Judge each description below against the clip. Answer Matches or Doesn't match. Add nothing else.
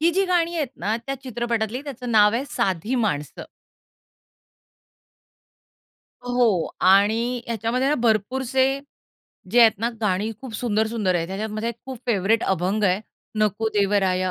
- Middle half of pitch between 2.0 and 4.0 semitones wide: Matches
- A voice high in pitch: Matches